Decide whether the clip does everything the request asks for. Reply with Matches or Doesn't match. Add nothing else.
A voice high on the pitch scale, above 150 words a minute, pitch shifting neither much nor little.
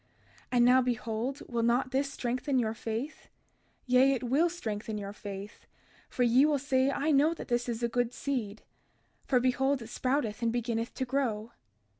Matches